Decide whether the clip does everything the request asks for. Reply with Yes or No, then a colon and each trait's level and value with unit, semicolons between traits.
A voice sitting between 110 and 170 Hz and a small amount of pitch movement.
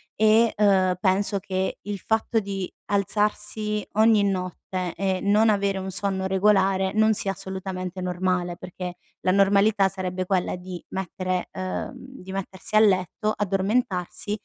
No: high, 195 Hz; narrow, 1.9 semitones